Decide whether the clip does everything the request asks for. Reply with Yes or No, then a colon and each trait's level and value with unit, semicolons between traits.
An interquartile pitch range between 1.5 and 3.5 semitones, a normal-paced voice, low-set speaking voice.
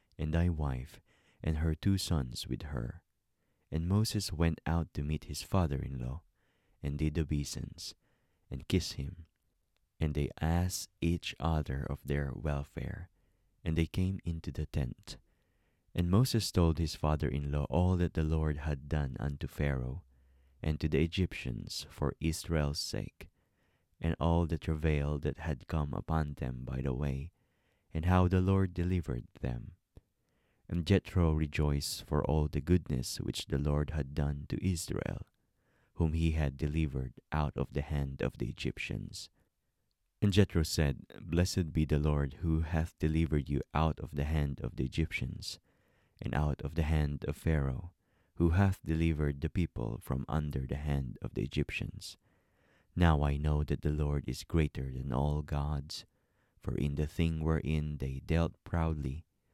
Yes: average, 2.9 semitones; average, 160 wpm; very low, 75 Hz